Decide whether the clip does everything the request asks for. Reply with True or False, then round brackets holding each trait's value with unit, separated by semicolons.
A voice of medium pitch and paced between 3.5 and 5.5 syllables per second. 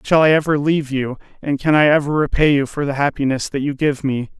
False (145 Hz; 6.0 syllables/s)